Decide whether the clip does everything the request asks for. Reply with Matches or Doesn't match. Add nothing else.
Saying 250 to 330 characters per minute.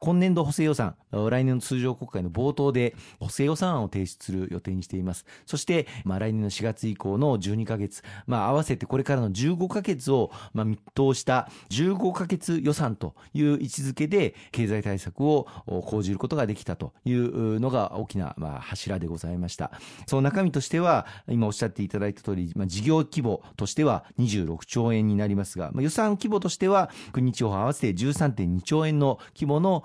Doesn't match